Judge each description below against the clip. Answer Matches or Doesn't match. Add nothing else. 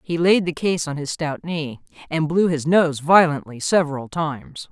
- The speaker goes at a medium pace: Matches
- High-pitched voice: Doesn't match